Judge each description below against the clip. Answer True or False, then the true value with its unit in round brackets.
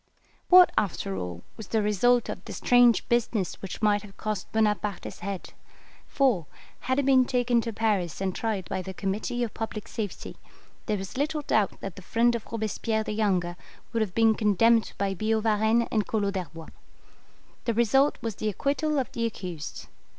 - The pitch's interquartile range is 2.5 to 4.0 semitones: True (3.2 semitones)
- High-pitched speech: True (215 Hz)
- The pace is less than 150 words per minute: False (180 wpm)